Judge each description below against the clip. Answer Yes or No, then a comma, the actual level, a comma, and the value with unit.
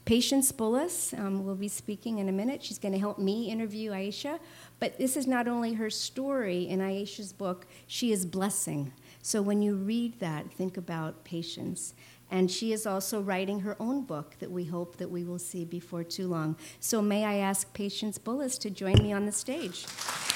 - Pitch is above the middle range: Yes, high, 200 Hz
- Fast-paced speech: No, average, 195 wpm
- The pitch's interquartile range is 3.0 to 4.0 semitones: Yes, average, 3.5 semitones